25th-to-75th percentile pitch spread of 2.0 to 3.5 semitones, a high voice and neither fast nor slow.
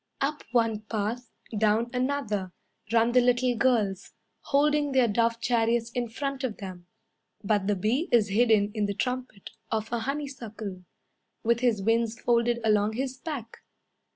Yes: average, 2.8 semitones; high, 230 Hz; average, 150 wpm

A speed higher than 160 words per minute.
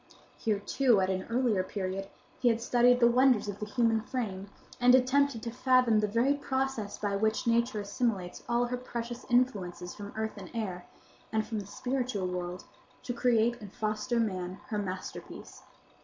Yes: average, 170 wpm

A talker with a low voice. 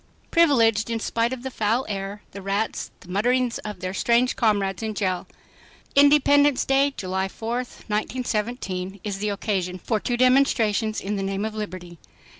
No: high, 215 Hz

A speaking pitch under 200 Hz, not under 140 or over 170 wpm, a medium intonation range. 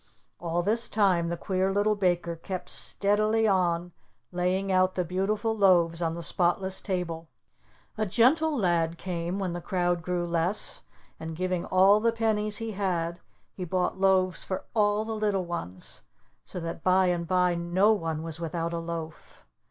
Yes: medium, 185 Hz; average, 165 wpm; average, 3.0 semitones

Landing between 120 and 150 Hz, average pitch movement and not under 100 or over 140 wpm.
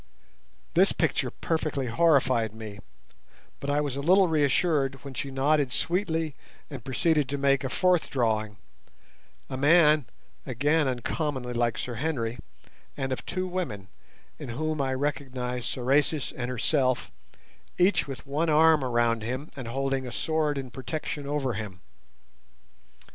Yes: low, 135 Hz; average, 3.8 semitones; slow, 135 wpm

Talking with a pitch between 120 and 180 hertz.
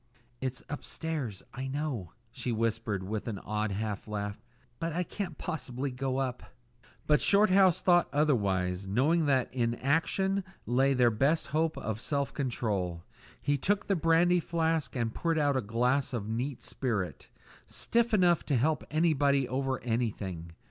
Yes: low, 135 Hz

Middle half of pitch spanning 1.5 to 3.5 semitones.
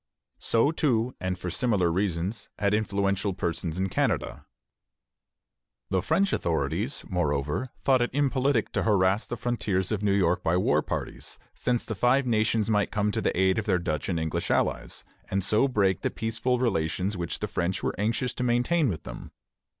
No: average, 4.7 semitones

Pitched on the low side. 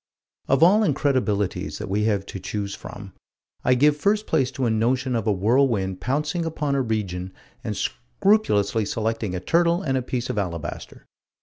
Yes: low, 115 Hz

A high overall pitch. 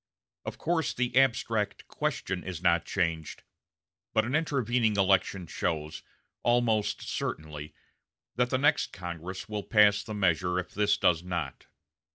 No: low, 100 Hz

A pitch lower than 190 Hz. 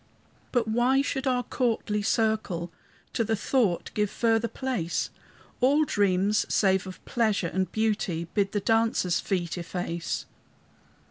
No: high, 215 Hz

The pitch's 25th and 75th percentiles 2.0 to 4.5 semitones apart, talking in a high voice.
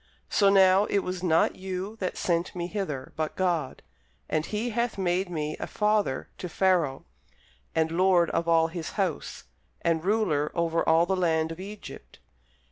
No: average, 3.0 semitones; medium, 180 Hz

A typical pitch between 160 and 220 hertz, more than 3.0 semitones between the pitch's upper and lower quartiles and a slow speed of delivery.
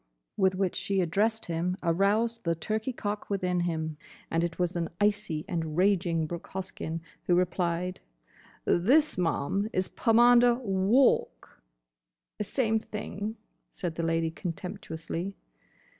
Yes: medium, 185 Hz; average, 3.9 semitones; slow, 125 wpm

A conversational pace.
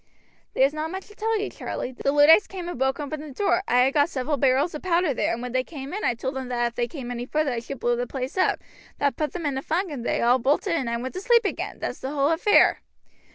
No: fast, 285 wpm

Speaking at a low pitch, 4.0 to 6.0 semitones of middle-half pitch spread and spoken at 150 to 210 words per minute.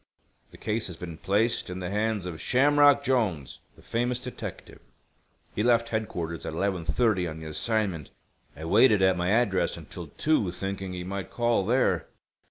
Yes: low, 100 Hz; average, 4.8 semitones; average, 165 wpm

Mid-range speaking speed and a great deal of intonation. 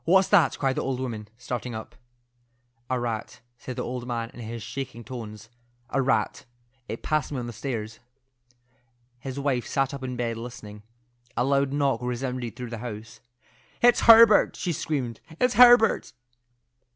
No: average, 155 wpm; average, 2.9 semitones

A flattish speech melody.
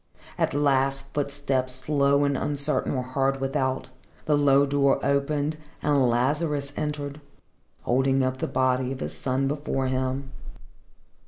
Yes: narrow, 1.5 semitones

